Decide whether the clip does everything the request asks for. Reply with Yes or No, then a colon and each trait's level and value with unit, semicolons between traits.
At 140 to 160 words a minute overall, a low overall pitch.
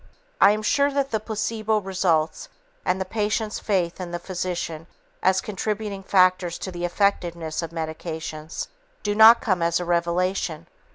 No: average, 155 wpm; medium, 185 Hz